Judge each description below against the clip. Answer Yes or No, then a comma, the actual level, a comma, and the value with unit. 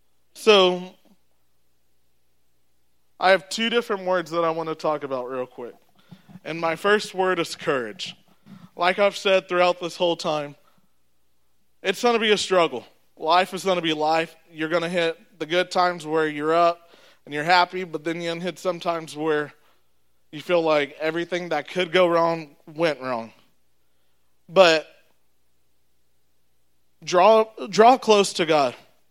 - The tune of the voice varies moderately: No, wide, 7.5 semitones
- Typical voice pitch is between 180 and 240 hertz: No, medium, 165 Hz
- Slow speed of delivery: No, average, 160 wpm